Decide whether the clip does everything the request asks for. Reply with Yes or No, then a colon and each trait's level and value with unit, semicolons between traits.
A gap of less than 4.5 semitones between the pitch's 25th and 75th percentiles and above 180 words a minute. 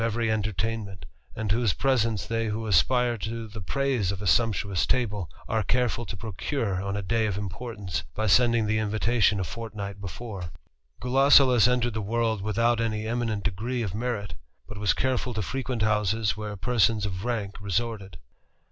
No: narrow, 2.6 semitones; average, 165 wpm